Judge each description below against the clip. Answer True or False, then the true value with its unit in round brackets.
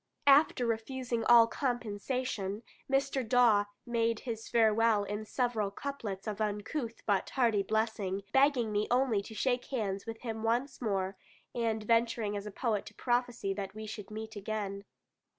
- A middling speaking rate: True (150 wpm)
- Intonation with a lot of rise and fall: False (2.7 semitones)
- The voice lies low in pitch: False (225 Hz)